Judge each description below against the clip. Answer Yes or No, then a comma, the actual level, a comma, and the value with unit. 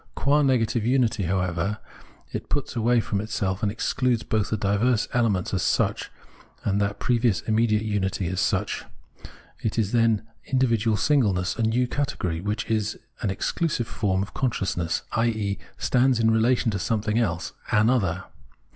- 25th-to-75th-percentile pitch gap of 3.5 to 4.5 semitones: No, average, 3.1 semitones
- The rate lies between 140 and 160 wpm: Yes, average, 155 wpm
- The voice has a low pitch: Yes, low, 110 Hz